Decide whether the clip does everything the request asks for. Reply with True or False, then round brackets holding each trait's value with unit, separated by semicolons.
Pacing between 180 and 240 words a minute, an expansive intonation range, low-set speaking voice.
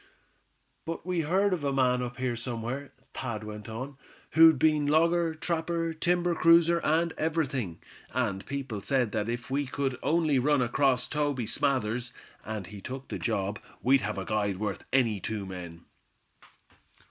False (160 wpm; 6.1 semitones; 130 Hz)